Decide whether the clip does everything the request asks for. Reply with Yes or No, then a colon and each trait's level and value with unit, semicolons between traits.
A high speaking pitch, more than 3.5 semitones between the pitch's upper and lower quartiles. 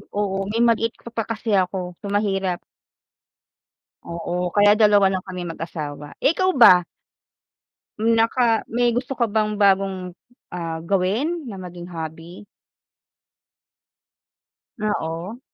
Yes: high, 195 Hz; average, 4.1 semitones